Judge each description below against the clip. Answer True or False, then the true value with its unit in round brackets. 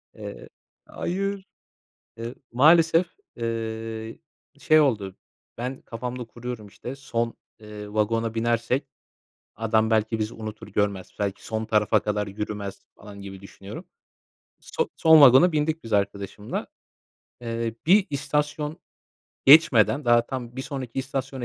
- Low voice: True (115 Hz)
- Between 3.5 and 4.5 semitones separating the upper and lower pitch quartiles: True (4.2 semitones)